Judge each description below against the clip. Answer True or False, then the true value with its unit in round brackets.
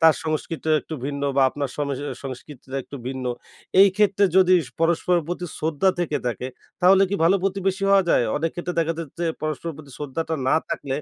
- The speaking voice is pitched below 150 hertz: False (160 Hz)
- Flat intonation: False (4.0 semitones)